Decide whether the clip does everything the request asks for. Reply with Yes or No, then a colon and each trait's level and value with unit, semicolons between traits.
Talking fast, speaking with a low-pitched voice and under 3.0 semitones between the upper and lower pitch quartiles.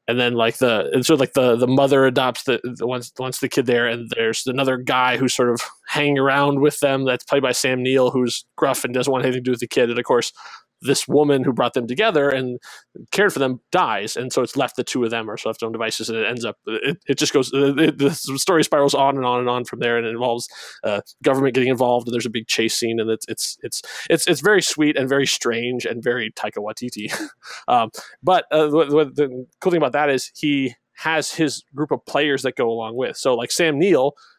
Yes: fast, 250 wpm; low, 130 Hz; narrow, 2.5 semitones